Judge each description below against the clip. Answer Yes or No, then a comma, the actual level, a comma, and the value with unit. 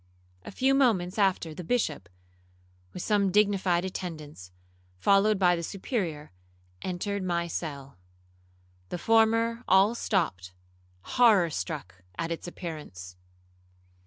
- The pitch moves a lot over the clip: No, average, 4.9 semitones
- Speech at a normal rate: No, slow, 110 wpm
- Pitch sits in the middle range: Yes, medium, 180 Hz